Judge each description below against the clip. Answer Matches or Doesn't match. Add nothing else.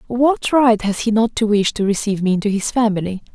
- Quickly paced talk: Matches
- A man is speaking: Doesn't match